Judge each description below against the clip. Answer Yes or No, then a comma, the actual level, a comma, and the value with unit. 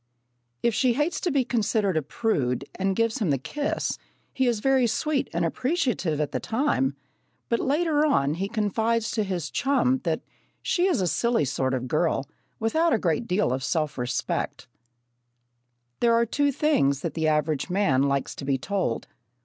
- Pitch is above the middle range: Yes, high, 205 Hz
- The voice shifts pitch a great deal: Yes, wide, 8.8 semitones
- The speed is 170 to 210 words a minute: Yes, average, 180 wpm